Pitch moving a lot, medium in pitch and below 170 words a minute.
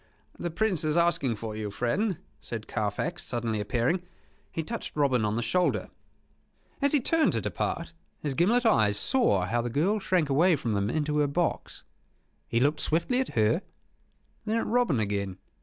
No: wide, 8.3 semitones; medium, 150 Hz; average, 175 wpm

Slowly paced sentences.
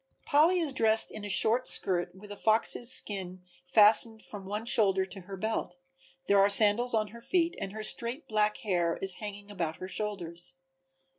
No: average, 180 wpm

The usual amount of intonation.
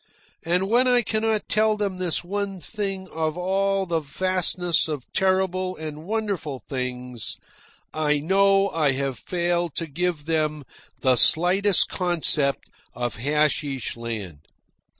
Yes: average, 4.6 semitones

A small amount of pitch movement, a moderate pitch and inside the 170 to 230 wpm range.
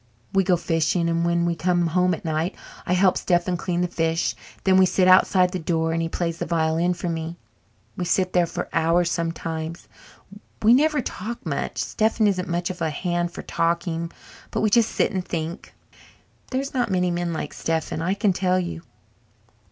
Yes: narrow, 1.9 semitones; medium, 175 Hz; average, 195 wpm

